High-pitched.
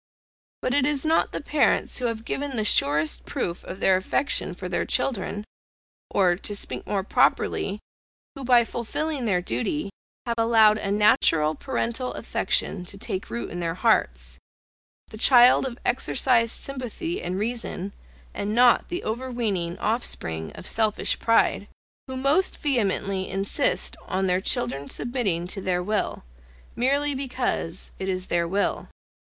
Yes: high, 215 Hz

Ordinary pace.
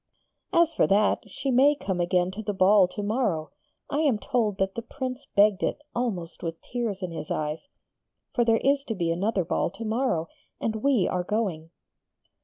Yes: average, 190 wpm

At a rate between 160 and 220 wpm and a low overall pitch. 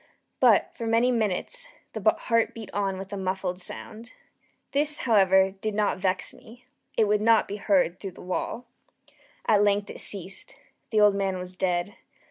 No: average, 170 wpm; high, 205 Hz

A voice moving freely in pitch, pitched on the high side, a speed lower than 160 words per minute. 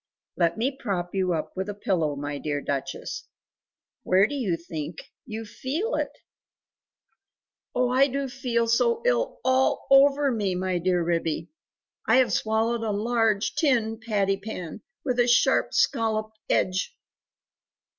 Yes: wide, 5.8 semitones; high, 220 Hz; average, 145 wpm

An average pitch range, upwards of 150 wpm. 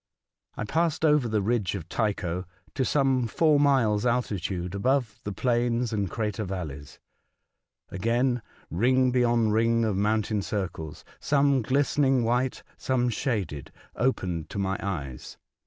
No: average, 4.7 semitones; average, 140 wpm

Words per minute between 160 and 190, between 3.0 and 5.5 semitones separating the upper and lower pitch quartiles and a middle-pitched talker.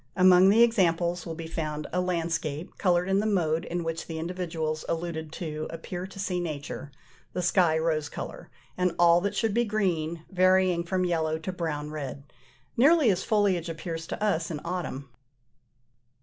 No: average, 170 wpm; narrow, 2.6 semitones; medium, 170 Hz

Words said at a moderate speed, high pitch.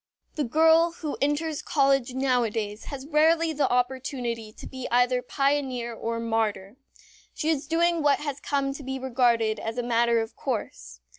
Yes: average, 160 wpm; very high, 260 Hz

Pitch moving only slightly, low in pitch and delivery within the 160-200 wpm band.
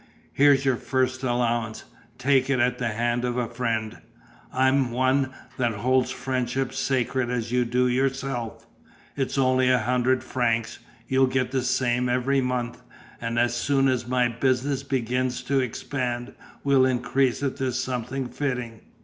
No: narrow, 1.5 semitones; low, 125 Hz; average, 150 wpm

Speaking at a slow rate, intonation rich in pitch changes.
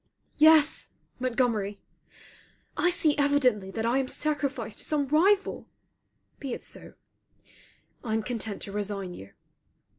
Yes: slow, 125 wpm; wide, 5.8 semitones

